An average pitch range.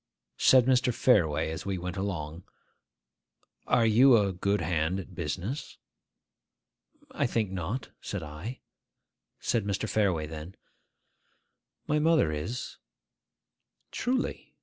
No: wide, 6.6 semitones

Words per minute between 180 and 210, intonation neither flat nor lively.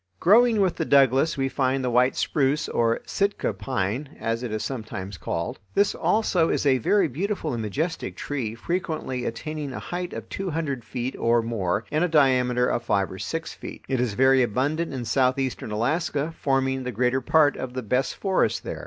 Yes: average, 190 wpm; average, 4.7 semitones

